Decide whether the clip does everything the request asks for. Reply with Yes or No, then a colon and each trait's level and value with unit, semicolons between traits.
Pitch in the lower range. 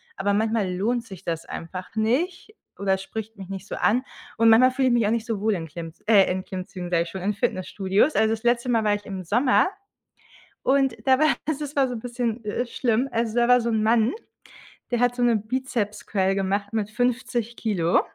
No: high, 220 Hz